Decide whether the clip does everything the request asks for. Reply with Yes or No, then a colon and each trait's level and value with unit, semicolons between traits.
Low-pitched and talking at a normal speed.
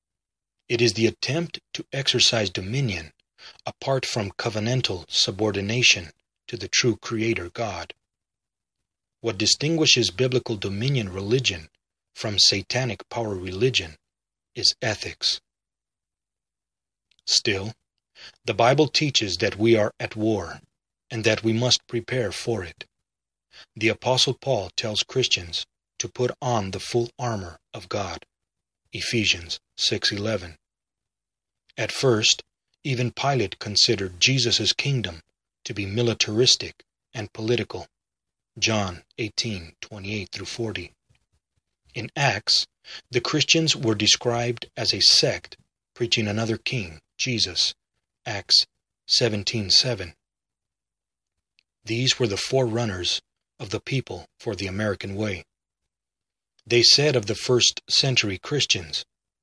No: low, 115 Hz; slow, 110 wpm